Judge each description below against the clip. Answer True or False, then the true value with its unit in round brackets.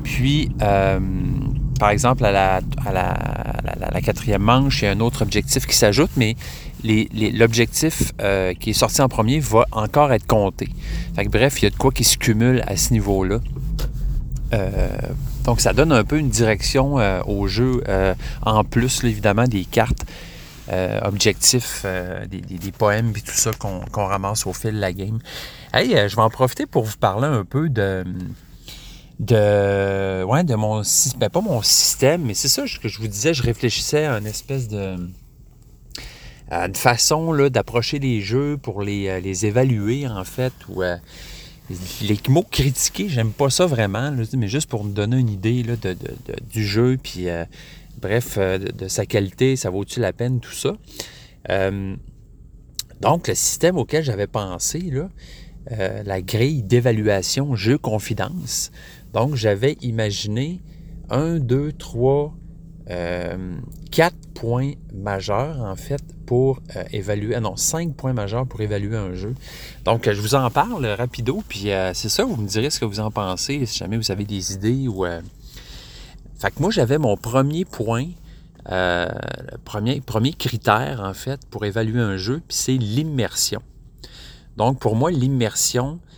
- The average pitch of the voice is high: False (115 Hz)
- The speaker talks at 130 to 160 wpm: False (180 wpm)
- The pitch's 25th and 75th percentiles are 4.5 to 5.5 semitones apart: True (4.8 semitones)